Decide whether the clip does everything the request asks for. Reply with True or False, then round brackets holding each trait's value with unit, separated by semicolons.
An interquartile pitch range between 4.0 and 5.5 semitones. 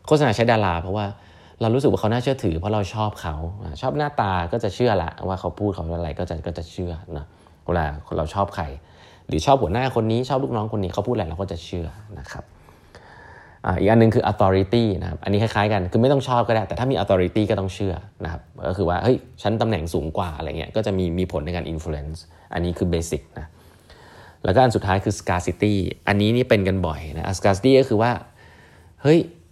True (4.6 semitones)